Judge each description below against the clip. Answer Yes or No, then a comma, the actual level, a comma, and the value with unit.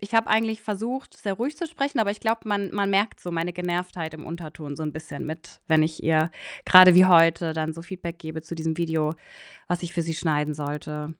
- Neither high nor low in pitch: Yes, medium, 170 Hz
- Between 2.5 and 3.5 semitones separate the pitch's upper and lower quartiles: No, average, 4.0 semitones